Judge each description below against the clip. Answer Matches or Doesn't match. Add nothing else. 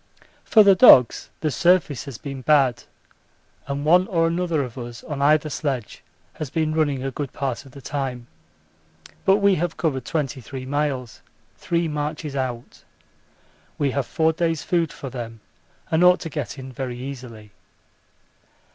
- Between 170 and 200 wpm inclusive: Doesn't match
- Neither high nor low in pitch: Matches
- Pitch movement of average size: Matches